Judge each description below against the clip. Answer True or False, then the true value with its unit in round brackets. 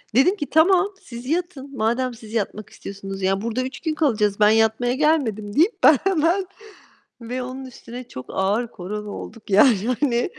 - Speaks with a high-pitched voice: True (245 Hz)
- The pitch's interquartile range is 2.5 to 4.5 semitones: False (5.6 semitones)